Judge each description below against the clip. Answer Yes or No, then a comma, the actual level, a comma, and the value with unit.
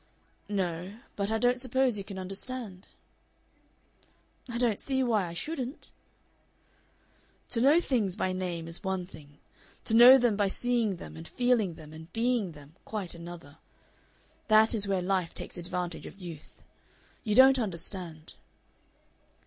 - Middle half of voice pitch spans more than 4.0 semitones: Yes, wide, 5.6 semitones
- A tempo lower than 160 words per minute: Yes, average, 145 wpm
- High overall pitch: Yes, high, 195 Hz